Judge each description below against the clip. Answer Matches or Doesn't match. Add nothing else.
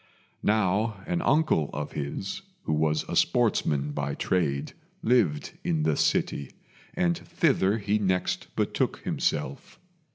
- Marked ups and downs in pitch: Matches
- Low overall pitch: Matches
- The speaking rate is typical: Doesn't match